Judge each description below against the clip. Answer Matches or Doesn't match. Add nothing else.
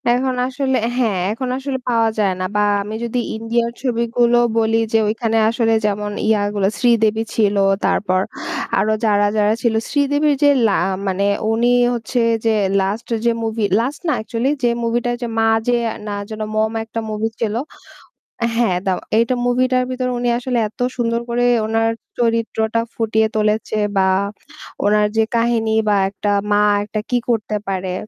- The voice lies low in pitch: Doesn't match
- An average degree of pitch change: Doesn't match